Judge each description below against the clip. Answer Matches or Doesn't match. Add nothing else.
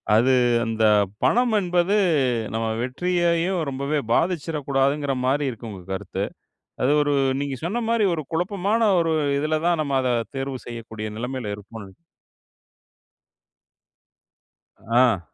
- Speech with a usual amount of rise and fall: Doesn't match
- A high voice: Doesn't match